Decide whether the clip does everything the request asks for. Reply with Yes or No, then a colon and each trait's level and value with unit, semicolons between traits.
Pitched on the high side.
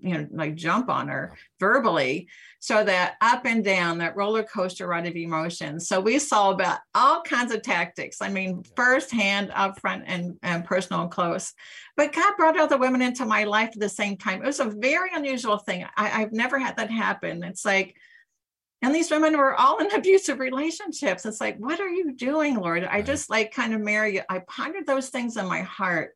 Yes: high, 220 Hz